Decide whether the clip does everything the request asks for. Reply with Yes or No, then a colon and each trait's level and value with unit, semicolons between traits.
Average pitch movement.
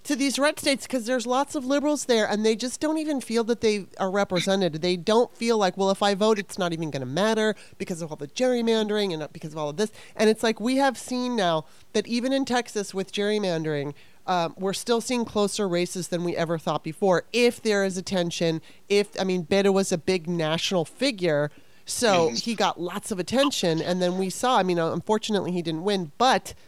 Yes: average, 4.9 semitones